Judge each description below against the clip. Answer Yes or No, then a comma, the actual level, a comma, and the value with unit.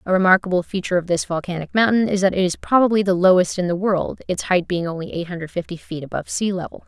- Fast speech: Yes, fast, 245 wpm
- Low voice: No, medium, 185 Hz